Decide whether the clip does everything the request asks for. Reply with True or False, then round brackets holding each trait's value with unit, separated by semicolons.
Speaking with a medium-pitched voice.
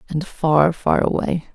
True (160 Hz)